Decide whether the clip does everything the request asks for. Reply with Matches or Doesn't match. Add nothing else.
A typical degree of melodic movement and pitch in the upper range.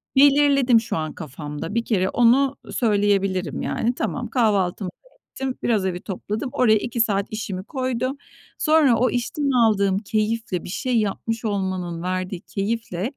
Matches